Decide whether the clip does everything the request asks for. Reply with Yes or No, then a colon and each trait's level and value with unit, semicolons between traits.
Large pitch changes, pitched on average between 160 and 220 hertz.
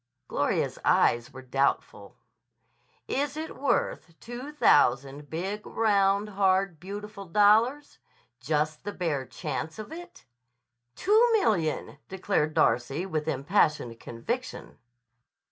Yes: wide, 6.2 semitones; high, 190 Hz